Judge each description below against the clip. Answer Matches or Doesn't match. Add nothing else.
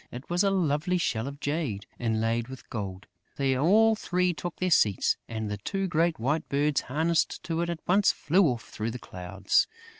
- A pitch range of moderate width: Doesn't match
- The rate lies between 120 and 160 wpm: Doesn't match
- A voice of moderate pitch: Matches